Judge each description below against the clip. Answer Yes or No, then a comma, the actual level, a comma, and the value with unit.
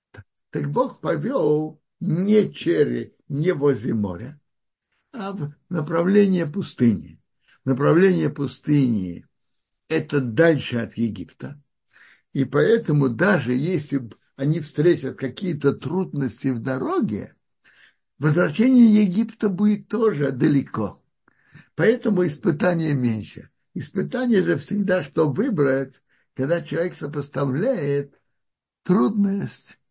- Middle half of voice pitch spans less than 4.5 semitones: No, wide, 5.4 semitones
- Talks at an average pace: No, slow, 90 wpm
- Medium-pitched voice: Yes, medium, 150 Hz